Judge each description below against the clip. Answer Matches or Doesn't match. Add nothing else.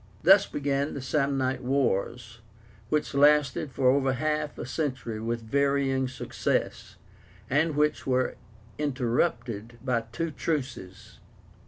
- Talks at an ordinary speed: Doesn't match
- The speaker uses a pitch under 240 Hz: Matches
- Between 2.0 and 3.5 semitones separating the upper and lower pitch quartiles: Matches